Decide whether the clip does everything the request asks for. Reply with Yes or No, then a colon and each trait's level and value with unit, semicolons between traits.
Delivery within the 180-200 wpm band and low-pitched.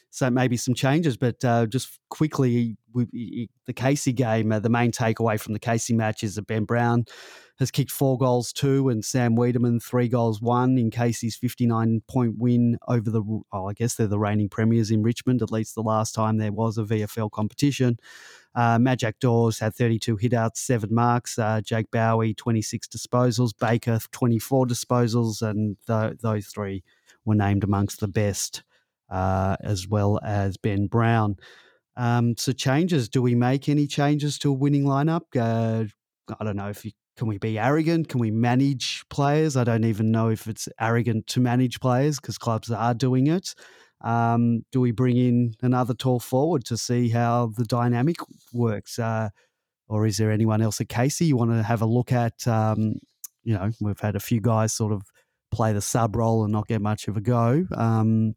Yes: average, 190 wpm; low, 115 Hz